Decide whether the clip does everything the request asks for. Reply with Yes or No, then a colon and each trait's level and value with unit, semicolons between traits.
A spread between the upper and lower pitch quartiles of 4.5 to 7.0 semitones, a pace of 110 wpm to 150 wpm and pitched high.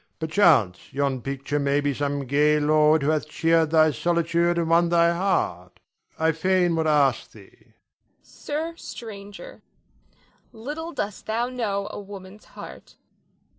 No: average, 5.2 semitones; average, 140 wpm; medium, 165 Hz